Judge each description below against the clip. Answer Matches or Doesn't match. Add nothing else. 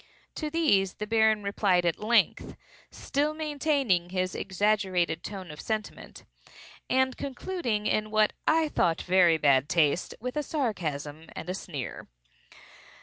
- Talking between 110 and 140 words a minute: Matches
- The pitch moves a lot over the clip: Matches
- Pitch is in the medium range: Doesn't match